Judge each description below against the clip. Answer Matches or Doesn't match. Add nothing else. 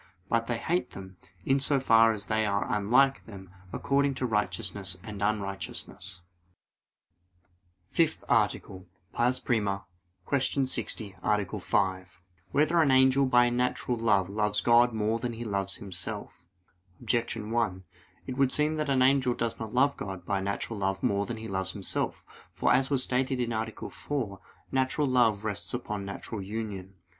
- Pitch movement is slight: Doesn't match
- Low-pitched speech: Matches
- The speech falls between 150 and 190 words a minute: Matches